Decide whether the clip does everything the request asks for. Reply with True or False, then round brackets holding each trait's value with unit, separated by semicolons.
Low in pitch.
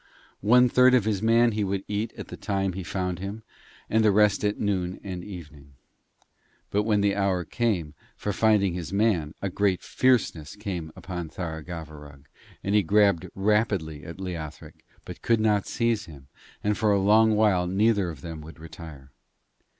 True (95 Hz)